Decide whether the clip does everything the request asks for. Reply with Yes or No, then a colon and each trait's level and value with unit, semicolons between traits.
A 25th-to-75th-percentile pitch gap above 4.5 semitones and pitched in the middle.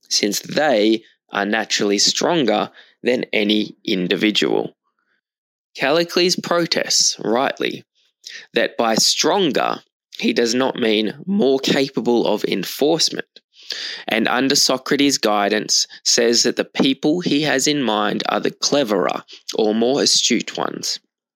No: wide, 5.4 semitones; low, 120 Hz